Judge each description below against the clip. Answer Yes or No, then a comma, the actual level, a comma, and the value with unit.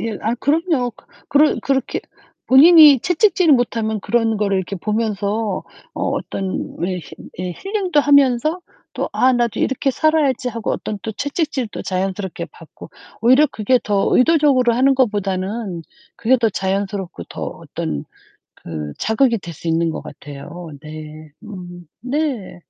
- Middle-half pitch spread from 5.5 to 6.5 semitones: Yes, wide, 6.2 semitones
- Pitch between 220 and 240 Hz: Yes, high, 225 Hz